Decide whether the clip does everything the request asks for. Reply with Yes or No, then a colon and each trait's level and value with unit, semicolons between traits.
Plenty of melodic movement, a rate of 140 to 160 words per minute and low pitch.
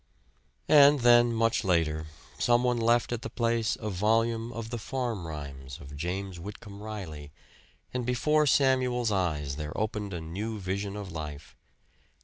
Yes: wide, 6.1 semitones; average, 150 wpm; low, 105 Hz